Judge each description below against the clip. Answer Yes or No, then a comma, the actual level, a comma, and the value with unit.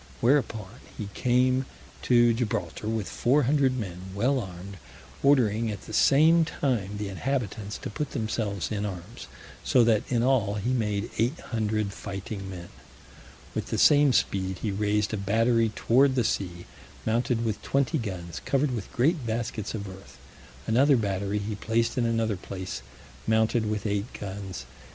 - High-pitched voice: No, low, 110 Hz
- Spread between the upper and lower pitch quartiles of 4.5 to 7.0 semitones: No, average, 3.7 semitones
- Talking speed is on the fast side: No, average, 155 wpm